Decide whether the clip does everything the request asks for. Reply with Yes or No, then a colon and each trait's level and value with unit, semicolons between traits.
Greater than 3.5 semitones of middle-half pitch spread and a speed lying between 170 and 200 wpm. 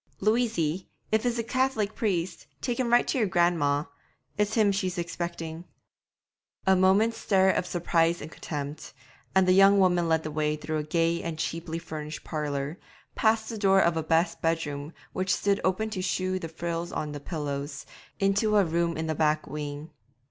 Yes: average, 3.9 semitones; average, 185 wpm